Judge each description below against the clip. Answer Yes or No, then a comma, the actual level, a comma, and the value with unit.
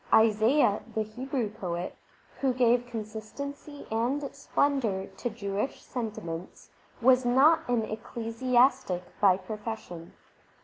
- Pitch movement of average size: Yes, average, 3.6 semitones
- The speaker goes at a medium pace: No, slow, 100 wpm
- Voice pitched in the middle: No, high, 230 Hz